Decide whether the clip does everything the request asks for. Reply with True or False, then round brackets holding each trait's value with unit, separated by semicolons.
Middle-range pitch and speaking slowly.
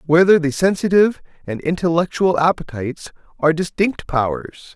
True (165 Hz; 115 wpm)